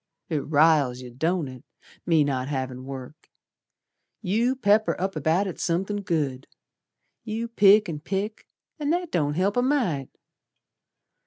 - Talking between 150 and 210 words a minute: No, average, 140 wpm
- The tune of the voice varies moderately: No, wide, 6.6 semitones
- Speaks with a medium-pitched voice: Yes, medium, 170 Hz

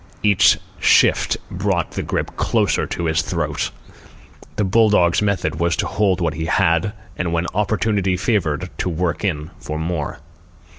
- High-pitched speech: No, very low, 90 Hz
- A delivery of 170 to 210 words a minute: No, average, 155 wpm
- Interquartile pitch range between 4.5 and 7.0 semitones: No, average, 3.5 semitones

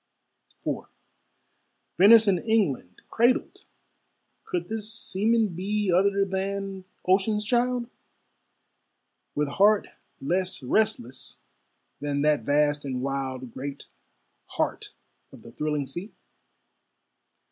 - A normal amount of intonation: No, wide, 6.7 semitones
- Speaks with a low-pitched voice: No, high, 190 Hz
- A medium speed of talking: No, slow, 95 wpm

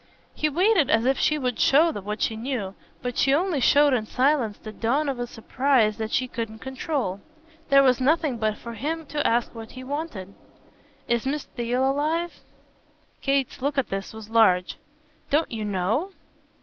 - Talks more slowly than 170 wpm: No, average, 175 wpm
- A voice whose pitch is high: Yes, very high, 255 Hz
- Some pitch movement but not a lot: Yes, average, 4.5 semitones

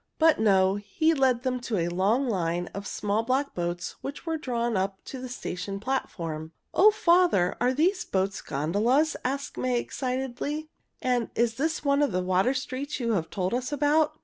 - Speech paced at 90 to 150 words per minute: No, average, 180 wpm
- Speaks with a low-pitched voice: No, high, 245 Hz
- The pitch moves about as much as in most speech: No, wide, 6.5 semitones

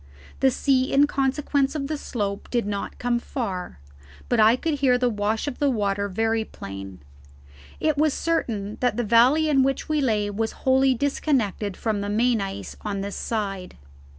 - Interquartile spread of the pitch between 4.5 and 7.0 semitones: Yes, average, 4.8 semitones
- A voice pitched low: No, high, 235 Hz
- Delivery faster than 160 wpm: Yes, average, 180 wpm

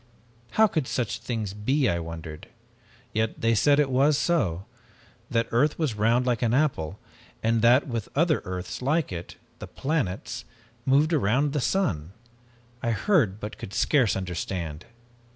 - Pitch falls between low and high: No, low, 115 Hz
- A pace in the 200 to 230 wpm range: No, average, 155 wpm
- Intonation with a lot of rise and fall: Yes, wide, 6.8 semitones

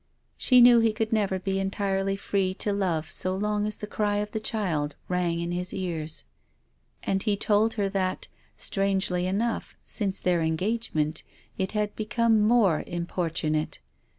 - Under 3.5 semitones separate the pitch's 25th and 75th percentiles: Yes, average, 2.9 semitones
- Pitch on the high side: Yes, high, 195 Hz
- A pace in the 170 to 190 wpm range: No, average, 155 wpm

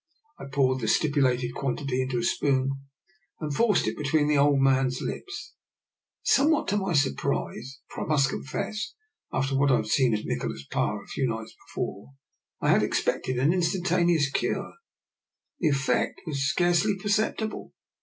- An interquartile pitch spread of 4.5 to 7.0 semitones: Yes, average, 4.9 semitones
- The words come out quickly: No, average, 165 wpm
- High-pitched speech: No, medium, 140 Hz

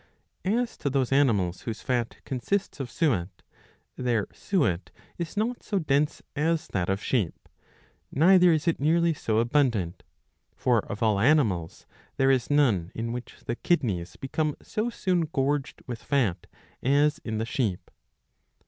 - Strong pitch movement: Yes, wide, 6.0 semitones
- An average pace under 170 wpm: Yes, average, 150 wpm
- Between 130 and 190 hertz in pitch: Yes, low, 135 Hz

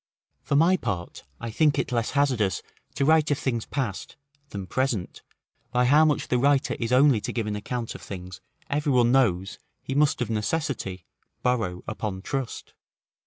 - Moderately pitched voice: No, low, 125 Hz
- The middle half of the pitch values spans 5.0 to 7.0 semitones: Yes, average, 5.3 semitones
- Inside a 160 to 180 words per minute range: Yes, average, 170 wpm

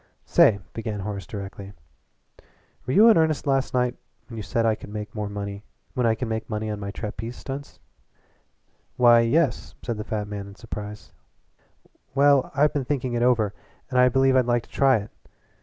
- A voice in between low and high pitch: No, low, 115 Hz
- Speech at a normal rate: Yes, average, 165 wpm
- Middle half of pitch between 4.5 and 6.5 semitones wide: No, average, 3.7 semitones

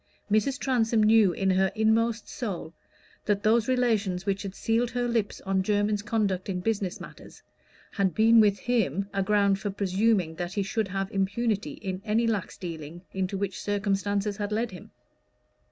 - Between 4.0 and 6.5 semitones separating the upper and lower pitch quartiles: No, narrow, 2.6 semitones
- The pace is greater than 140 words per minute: Yes, average, 170 wpm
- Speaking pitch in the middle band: No, high, 205 Hz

